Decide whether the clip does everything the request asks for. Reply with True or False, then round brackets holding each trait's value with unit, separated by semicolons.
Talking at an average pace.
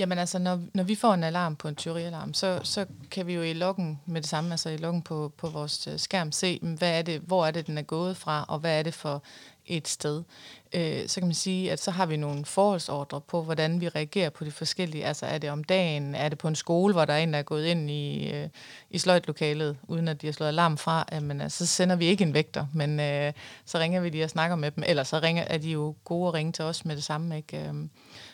False (260 wpm)